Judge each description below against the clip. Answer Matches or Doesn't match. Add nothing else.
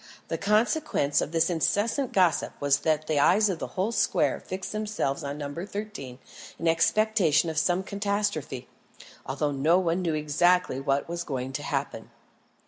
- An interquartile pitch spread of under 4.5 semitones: Doesn't match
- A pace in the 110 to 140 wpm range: Doesn't match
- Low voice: Doesn't match